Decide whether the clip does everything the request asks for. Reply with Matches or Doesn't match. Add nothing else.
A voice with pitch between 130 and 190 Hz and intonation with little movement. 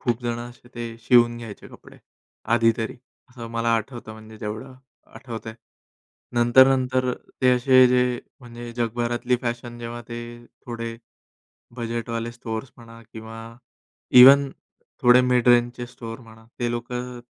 Doesn't match